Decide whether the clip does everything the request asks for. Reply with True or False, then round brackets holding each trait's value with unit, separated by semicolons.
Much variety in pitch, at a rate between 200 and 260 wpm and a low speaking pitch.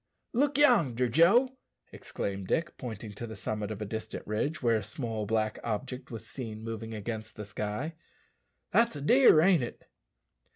False (6.6 semitones; 165 wpm; 115 Hz)